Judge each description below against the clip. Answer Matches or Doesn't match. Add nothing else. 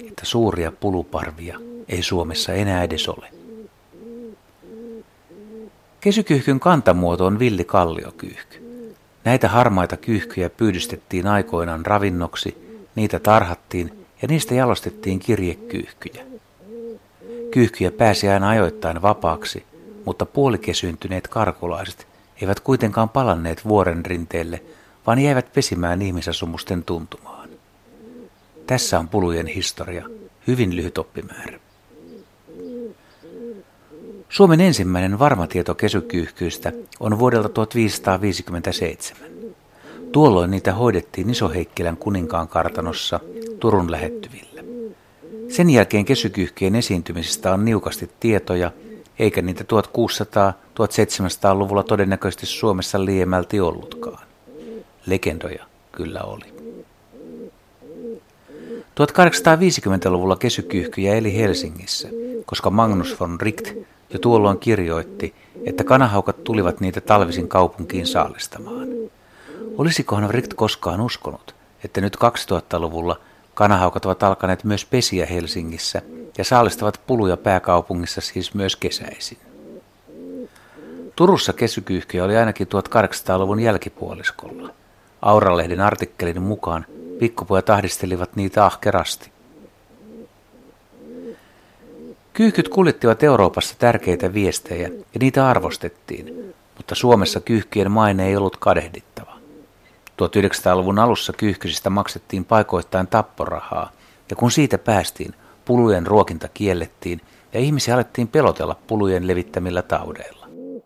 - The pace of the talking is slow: Matches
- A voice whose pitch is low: Matches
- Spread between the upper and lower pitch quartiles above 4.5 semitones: Matches